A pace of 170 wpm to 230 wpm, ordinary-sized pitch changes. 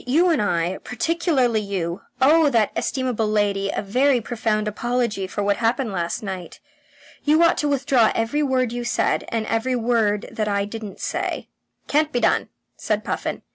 Yes: average, 175 wpm; average, 4.0 semitones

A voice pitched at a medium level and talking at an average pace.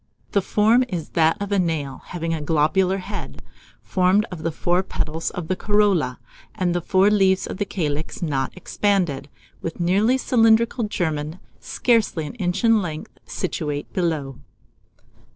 Yes: medium, 180 Hz; average, 150 wpm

